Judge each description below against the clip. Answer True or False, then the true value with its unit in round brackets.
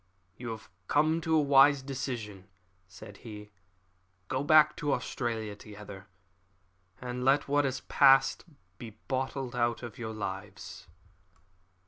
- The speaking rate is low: True (125 wpm)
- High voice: False (125 Hz)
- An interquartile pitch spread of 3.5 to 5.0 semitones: True (4.3 semitones)